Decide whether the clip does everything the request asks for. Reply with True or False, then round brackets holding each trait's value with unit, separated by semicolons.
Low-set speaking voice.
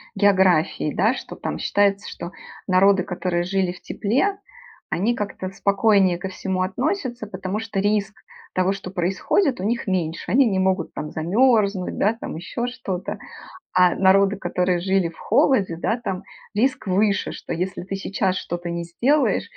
False (195 Hz)